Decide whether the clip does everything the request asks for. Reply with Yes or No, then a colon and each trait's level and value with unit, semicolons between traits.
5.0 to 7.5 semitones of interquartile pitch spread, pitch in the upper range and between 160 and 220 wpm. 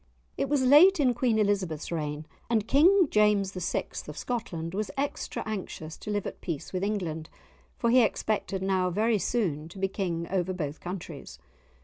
Yes: average, 5.3 semitones; high, 195 Hz; average, 170 wpm